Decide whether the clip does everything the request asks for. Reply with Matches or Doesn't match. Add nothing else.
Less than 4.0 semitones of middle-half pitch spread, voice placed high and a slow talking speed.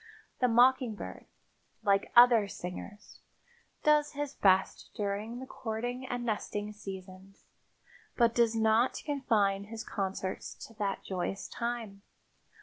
Matches